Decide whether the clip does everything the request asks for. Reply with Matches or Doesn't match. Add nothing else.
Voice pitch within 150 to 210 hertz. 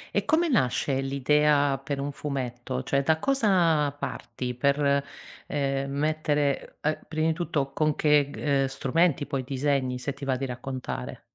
Doesn't match